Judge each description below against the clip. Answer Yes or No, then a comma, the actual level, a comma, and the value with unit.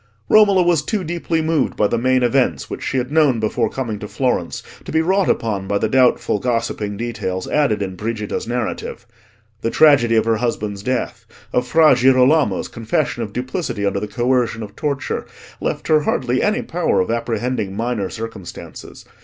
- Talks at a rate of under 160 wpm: No, average, 175 wpm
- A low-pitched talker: Yes, low, 120 Hz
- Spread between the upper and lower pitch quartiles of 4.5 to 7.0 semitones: Yes, average, 4.9 semitones